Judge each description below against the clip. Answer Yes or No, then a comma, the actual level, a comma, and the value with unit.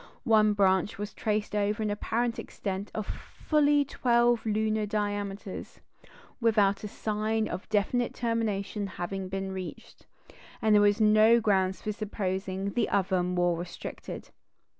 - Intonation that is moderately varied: No, narrow, 2.1 semitones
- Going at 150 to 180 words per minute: No, slow, 135 wpm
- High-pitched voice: Yes, high, 210 Hz